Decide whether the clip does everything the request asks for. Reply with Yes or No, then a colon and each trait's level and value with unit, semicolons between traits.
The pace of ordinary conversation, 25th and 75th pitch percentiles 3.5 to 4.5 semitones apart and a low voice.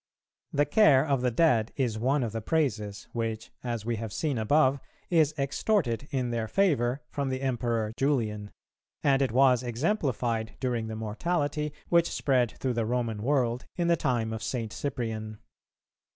Yes: average, 165 wpm; average, 4.1 semitones; low, 125 Hz